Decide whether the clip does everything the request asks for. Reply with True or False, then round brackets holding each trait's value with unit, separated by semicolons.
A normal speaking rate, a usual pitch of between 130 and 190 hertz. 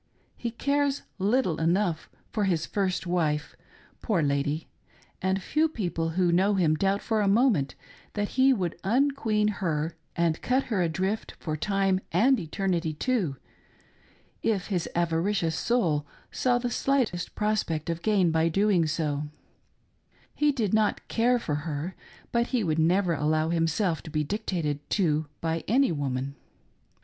True (150 wpm; 185 Hz)